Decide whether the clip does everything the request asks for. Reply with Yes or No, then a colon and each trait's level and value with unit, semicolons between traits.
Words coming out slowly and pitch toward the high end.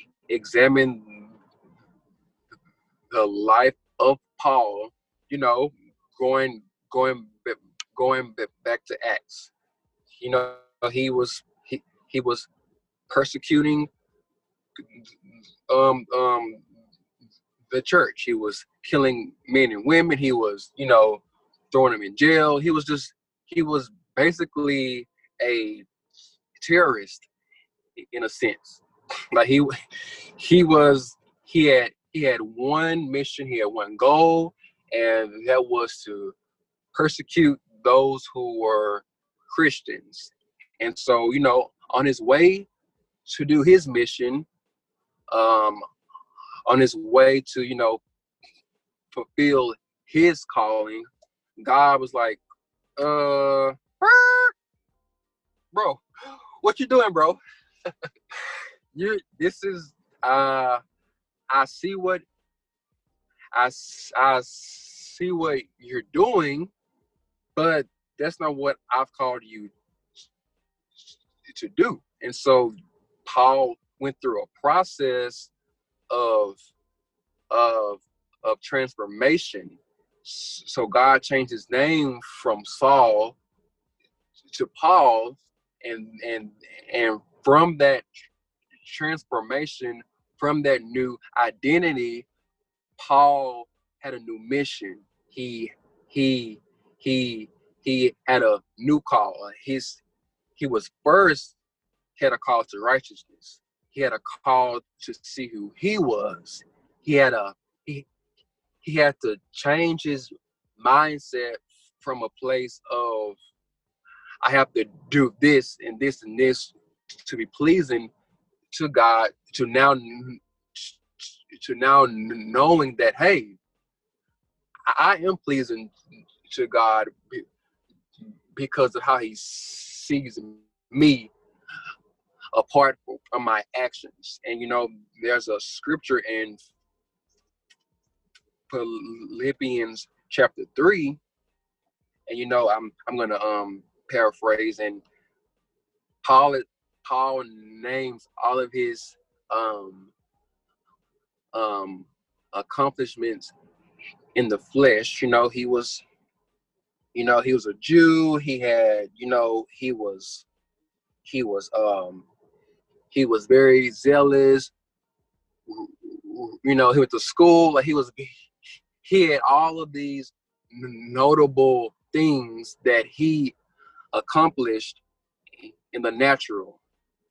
No: slow, 105 wpm; low, 135 Hz